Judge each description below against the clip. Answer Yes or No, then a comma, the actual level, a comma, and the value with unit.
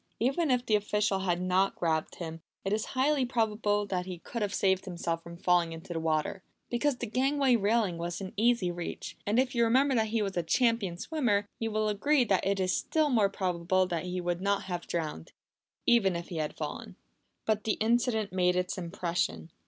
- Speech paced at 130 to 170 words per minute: No, fast, 205 wpm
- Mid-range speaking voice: No, high, 200 Hz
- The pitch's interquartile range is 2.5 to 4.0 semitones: No, average, 4.7 semitones